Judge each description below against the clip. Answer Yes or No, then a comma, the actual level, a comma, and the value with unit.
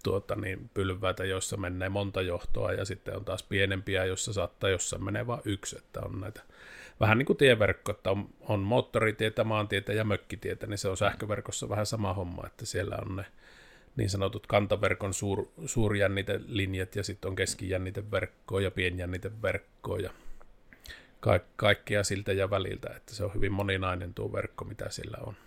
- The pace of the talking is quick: Yes, fast, 165 wpm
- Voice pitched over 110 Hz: No, low, 100 Hz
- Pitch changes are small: Yes, narrow, 1.6 semitones